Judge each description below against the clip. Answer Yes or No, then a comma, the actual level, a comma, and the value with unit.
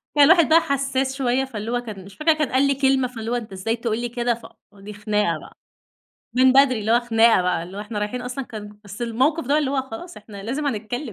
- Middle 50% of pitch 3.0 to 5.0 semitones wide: Yes, average, 4.2 semitones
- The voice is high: Yes, high, 240 Hz